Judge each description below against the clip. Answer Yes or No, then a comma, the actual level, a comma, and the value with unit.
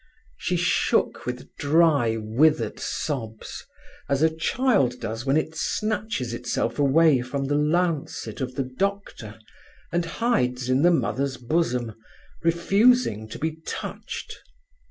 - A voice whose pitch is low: No, medium, 145 Hz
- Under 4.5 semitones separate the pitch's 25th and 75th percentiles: No, average, 5.2 semitones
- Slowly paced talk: Yes, slow, 125 wpm